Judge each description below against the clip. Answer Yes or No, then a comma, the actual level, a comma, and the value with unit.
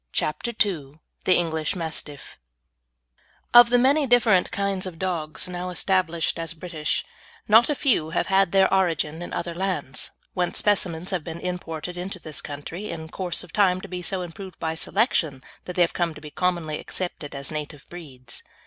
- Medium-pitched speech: Yes, medium, 175 Hz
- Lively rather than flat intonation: No, average, 3.1 semitones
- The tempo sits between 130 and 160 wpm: No, average, 175 wpm